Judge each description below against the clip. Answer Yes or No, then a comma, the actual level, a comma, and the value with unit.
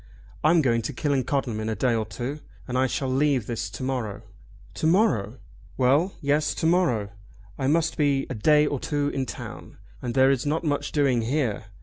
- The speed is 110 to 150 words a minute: No, average, 195 wpm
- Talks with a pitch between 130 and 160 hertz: Yes, low, 135 Hz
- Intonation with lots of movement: No, average, 3.7 semitones